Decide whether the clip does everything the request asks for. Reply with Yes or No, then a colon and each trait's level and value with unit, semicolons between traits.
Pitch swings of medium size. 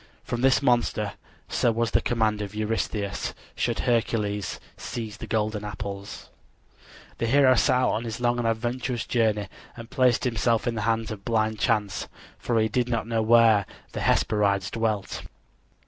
No: narrow, 2.1 semitones